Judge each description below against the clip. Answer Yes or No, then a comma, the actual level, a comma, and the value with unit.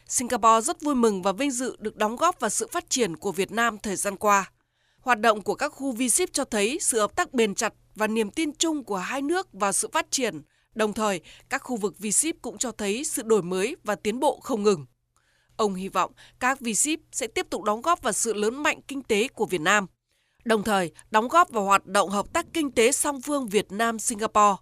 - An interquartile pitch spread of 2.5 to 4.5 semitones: No, average, 5.2 semitones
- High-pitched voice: Yes, high, 225 Hz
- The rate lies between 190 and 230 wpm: No, average, 240 wpm